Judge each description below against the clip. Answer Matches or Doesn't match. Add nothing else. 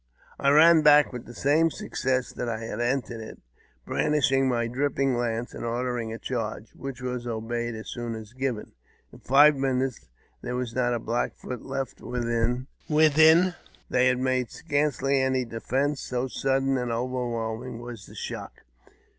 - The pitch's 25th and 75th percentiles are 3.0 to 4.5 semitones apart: Doesn't match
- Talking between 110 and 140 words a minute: Doesn't match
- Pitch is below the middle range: Matches